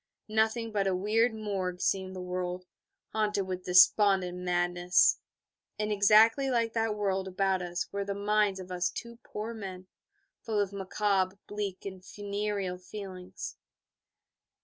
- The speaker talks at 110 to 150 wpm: Yes, average, 140 wpm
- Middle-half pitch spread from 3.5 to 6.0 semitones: No, narrow, 2.5 semitones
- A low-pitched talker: No, high, 195 Hz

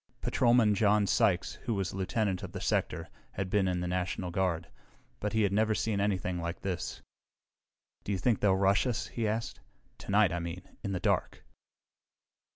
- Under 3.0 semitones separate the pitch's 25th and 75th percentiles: Yes, narrow, 2.5 semitones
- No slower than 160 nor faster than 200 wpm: Yes, average, 175 wpm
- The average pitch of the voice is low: Yes, low, 100 Hz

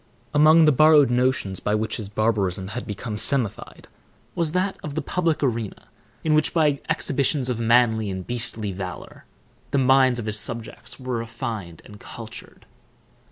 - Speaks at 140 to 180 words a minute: Yes, average, 160 wpm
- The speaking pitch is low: Yes, low, 120 Hz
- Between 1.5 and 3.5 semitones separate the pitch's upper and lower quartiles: No, average, 4.7 semitones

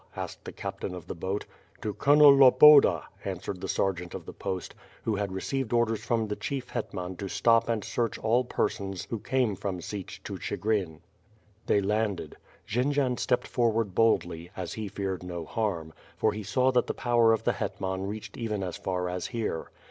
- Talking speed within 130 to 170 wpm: No, average, 185 wpm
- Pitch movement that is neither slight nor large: Yes, average, 4.1 semitones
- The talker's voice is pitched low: Yes, low, 105 Hz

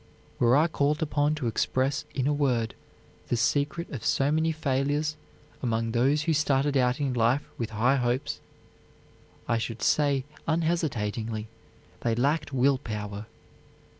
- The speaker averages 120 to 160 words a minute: Yes, average, 140 wpm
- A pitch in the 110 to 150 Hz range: Yes, low, 135 Hz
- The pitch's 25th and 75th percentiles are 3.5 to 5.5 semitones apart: Yes, average, 3.9 semitones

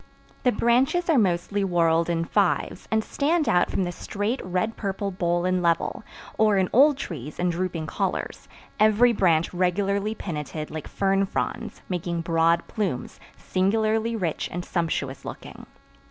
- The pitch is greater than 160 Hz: Yes, medium, 185 Hz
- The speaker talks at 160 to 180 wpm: No, average, 150 wpm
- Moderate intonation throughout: Yes, average, 4.2 semitones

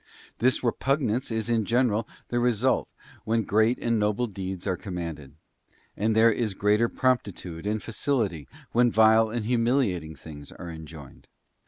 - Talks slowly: No, average, 145 wpm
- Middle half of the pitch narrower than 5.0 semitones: Yes, average, 4.2 semitones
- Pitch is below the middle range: Yes, low, 110 Hz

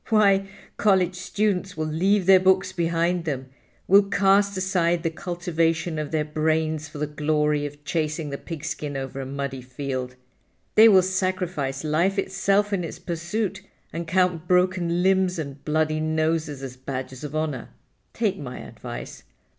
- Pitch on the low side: No, medium, 165 Hz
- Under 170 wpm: Yes, average, 155 wpm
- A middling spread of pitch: Yes, average, 3.8 semitones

